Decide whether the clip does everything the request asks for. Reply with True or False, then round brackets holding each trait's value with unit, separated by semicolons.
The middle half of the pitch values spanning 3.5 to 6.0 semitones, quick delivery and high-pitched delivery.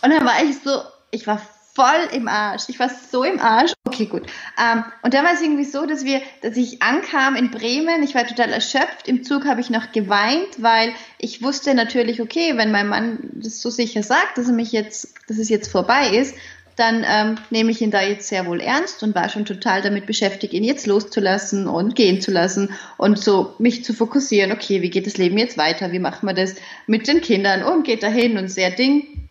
True (4.0 semitones; 225 wpm; 230 Hz)